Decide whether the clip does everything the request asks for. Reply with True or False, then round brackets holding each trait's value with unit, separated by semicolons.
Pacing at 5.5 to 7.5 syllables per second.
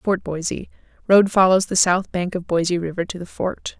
False (5.0 syllables/s)